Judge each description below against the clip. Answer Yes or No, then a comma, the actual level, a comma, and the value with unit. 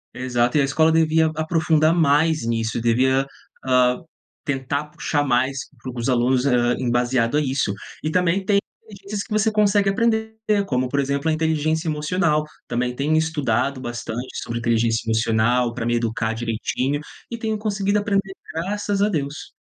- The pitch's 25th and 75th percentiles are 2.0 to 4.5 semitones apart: No, average, 5.1 semitones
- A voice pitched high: No, medium, 140 Hz